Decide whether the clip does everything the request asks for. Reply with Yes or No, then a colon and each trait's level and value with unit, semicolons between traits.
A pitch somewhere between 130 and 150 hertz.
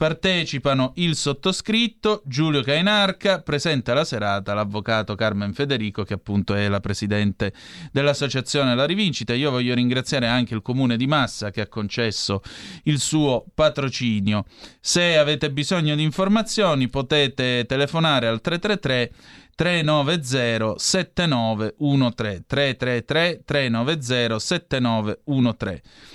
Yes: low, 135 Hz